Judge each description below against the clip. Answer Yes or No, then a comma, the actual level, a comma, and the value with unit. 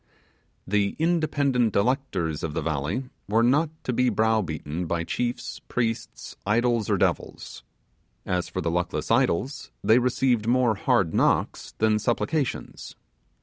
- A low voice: Yes, low, 110 Hz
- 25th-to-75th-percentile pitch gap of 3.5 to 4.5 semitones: No, wide, 5.6 semitones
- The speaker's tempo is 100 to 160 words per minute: Yes, slow, 135 wpm